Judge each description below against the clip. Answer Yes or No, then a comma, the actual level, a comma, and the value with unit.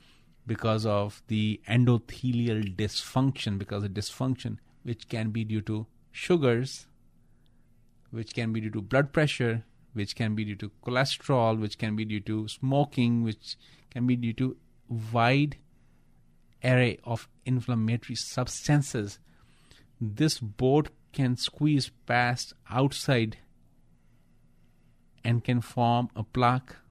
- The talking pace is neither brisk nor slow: No, slow, 120 wpm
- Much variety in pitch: No, average, 2.8 semitones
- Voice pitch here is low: Yes, low, 120 Hz